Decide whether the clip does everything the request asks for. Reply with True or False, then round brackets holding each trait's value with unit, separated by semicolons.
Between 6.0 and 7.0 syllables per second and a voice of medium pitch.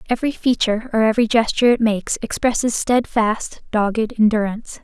False (6.1 syllables/s; 225 Hz)